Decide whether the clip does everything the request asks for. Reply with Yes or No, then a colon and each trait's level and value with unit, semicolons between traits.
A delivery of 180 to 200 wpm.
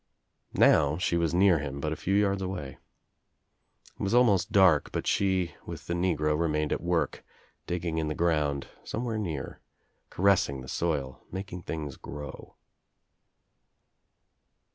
No: average, 145 wpm